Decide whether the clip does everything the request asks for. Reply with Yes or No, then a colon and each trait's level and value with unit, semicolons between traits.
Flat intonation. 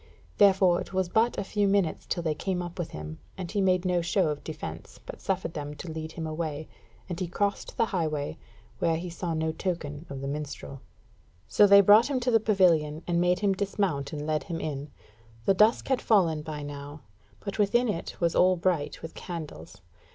No: average, 4.2 semitones